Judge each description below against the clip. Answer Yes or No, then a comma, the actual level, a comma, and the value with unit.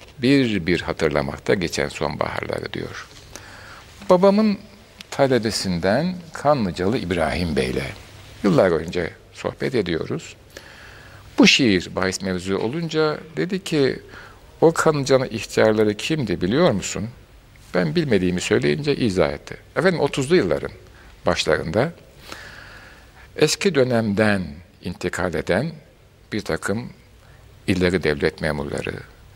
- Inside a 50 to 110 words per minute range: Yes, slow, 95 wpm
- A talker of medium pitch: No, low, 115 Hz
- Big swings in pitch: Yes, wide, 8.1 semitones